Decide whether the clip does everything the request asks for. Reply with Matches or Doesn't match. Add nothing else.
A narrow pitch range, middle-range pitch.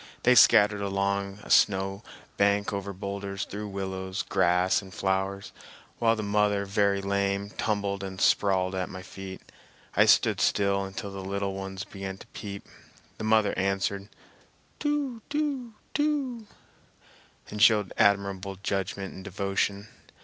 Doesn't match